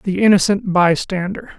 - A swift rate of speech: No, slow, 115 wpm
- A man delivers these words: Yes, male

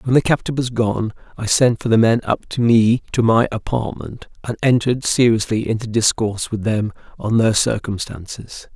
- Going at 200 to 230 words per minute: No, average, 180 wpm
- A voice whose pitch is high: No, low, 110 Hz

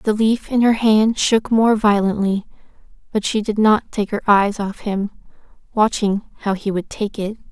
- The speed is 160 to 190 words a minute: Yes, average, 185 wpm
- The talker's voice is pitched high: Yes, high, 210 Hz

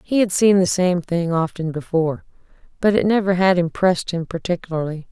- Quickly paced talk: No, average, 175 wpm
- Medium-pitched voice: Yes, medium, 180 Hz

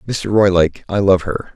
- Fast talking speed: No, average, 195 wpm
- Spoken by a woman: No, male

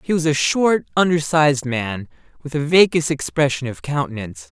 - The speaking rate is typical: Yes, average, 155 wpm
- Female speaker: No, male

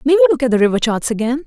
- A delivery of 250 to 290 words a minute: No, fast, 330 wpm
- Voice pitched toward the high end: Yes, very high, 255 Hz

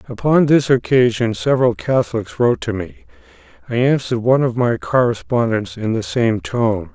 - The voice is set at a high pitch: No, low, 120 Hz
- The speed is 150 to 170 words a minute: Yes, average, 155 wpm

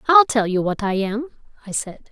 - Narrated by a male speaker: No, female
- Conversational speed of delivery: No, fast, 225 wpm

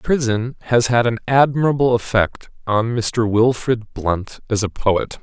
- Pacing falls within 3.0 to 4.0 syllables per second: Yes, 3.9 syllables/s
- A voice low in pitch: Yes, low, 115 Hz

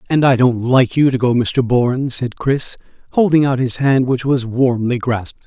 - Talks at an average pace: No, fast, 210 wpm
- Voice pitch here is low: Yes, low, 125 Hz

